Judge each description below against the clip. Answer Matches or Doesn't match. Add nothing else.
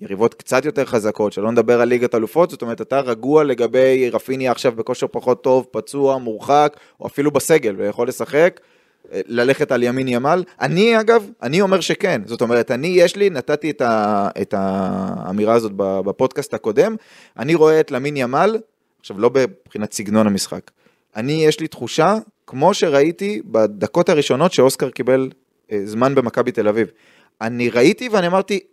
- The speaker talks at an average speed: Doesn't match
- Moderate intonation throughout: Doesn't match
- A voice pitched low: Matches